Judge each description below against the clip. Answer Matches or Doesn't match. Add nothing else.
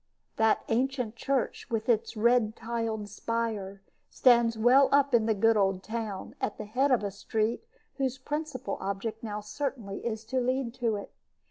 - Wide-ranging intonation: Doesn't match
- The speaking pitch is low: Doesn't match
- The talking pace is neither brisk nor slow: Matches